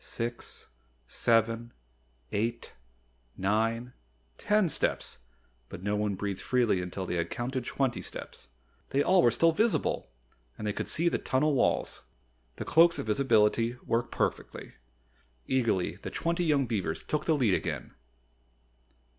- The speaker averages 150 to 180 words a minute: No, average, 140 wpm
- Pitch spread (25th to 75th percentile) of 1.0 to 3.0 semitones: No, average, 5.1 semitones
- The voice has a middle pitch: No, low, 120 Hz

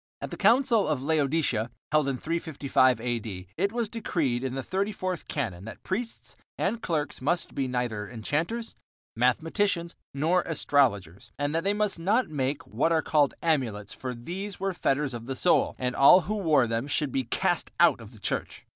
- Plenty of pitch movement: Yes, wide, 6.3 semitones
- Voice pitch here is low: No, medium, 145 Hz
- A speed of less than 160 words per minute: No, average, 180 wpm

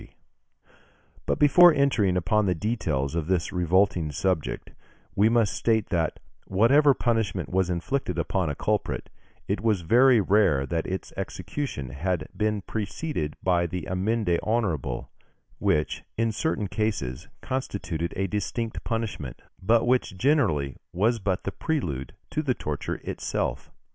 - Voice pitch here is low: Yes, low, 100 Hz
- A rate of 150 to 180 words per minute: No, average, 140 wpm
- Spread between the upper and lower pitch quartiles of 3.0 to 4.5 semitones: No, average, 5.2 semitones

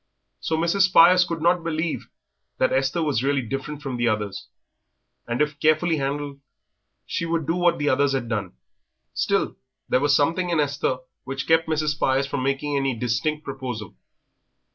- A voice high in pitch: No, medium, 145 Hz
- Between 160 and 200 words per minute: Yes, average, 165 wpm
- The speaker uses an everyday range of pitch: Yes, average, 3.5 semitones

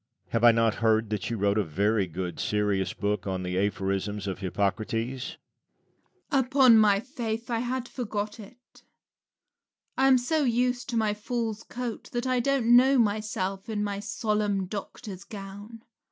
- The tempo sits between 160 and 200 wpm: Yes, average, 165 wpm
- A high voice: Yes, high, 205 Hz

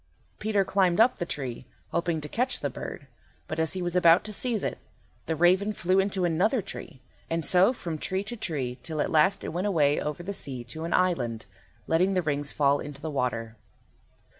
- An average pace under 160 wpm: No, fast, 205 wpm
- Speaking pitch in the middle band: Yes, medium, 170 Hz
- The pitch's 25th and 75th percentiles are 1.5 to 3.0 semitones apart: No, average, 4.6 semitones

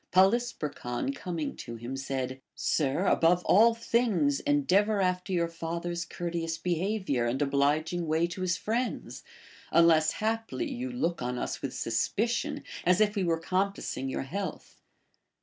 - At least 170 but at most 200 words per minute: No, average, 155 wpm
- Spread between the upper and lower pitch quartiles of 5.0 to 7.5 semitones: Yes, wide, 5.5 semitones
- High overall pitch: No, medium, 170 Hz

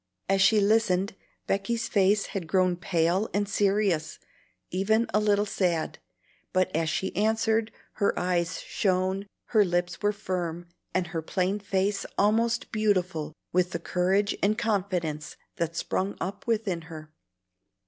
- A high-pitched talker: Yes, high, 195 Hz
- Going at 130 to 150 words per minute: Yes, average, 140 wpm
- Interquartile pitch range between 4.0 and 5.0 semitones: No, average, 2.8 semitones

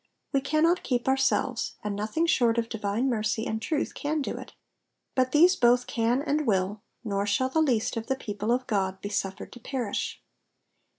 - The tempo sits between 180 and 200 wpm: Yes, average, 185 wpm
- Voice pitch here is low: No, high, 240 Hz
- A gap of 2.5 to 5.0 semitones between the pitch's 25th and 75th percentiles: Yes, average, 4.2 semitones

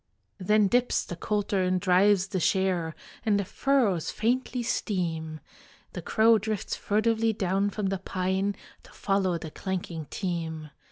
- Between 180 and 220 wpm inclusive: No, average, 145 wpm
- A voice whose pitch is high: Yes, high, 195 Hz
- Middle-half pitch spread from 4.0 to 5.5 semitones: No, average, 2.9 semitones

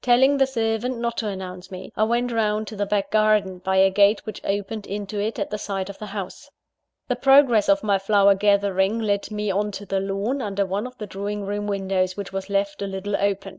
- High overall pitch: Yes, high, 205 Hz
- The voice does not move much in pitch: Yes, narrow, 1.8 semitones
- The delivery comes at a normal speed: No, fast, 230 wpm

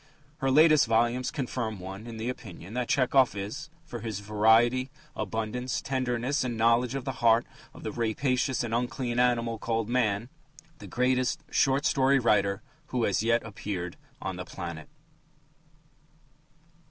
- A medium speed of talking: Yes, average, 145 wpm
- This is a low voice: Yes, low, 120 Hz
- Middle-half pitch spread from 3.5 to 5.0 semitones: No, average, 2.7 semitones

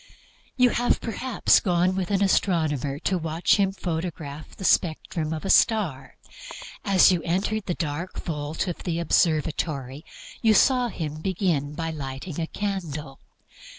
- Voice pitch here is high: No, medium, 170 Hz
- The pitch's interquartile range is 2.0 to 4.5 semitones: Yes, average, 4.1 semitones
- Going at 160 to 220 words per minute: No, average, 145 wpm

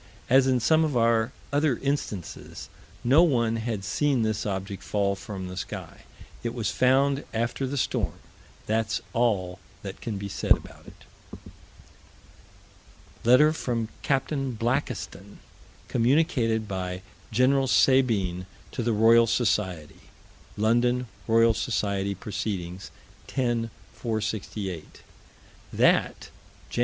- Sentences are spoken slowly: Yes, slow, 115 wpm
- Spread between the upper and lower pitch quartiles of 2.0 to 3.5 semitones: No, average, 4.2 semitones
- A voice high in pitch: No, low, 115 Hz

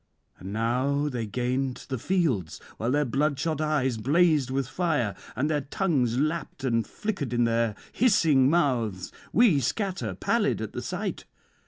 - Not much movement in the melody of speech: No, average, 4.7 semitones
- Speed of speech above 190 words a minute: No, average, 150 wpm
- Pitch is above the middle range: No, low, 135 Hz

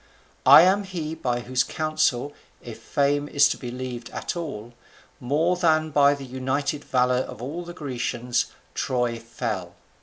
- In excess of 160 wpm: No, average, 155 wpm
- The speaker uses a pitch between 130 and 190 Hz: Yes, low, 135 Hz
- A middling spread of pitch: Yes, average, 4.1 semitones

